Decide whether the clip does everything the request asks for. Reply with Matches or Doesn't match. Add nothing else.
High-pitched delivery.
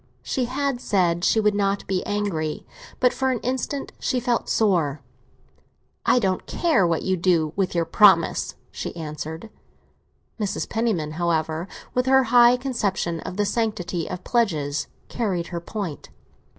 Matches